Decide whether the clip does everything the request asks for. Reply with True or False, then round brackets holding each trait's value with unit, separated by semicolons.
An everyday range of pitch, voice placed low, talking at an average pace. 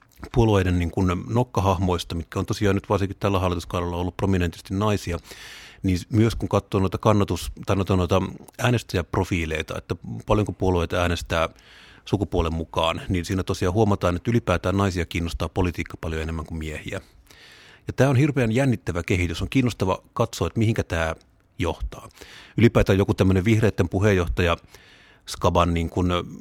True (3.3 semitones; 95 Hz; 140 wpm)